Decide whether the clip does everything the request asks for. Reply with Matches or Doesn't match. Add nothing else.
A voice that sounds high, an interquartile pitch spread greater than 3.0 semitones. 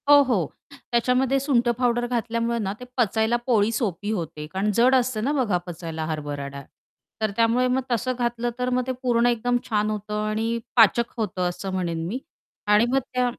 Matches